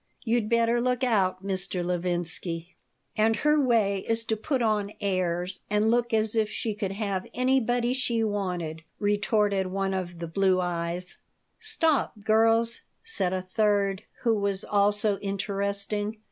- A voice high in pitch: Yes, high, 205 Hz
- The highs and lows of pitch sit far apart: No, average, 3.2 semitones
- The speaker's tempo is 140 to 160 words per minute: Yes, average, 145 wpm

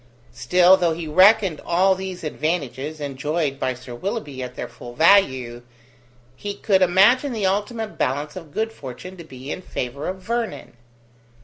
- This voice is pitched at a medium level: Yes, medium, 170 Hz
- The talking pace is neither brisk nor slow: Yes, average, 155 wpm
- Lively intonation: Yes, wide, 6.0 semitones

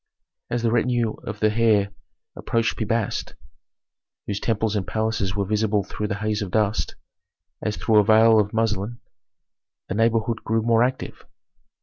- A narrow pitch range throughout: Yes, narrow, 1.6 semitones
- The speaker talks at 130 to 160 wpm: Yes, average, 155 wpm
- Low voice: Yes, low, 110 Hz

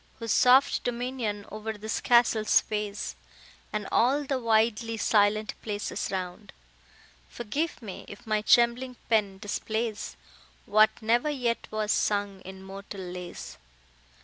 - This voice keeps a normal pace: No, slow, 120 wpm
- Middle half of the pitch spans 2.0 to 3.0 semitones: Yes, narrow, 2.6 semitones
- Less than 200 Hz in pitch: No, high, 215 Hz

